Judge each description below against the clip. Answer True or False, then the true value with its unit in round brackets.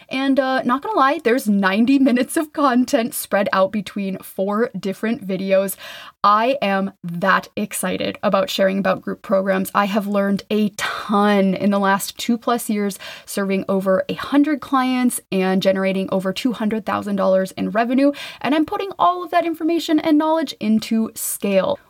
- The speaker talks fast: False (160 wpm)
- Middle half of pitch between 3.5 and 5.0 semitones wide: False (5.5 semitones)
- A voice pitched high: True (210 Hz)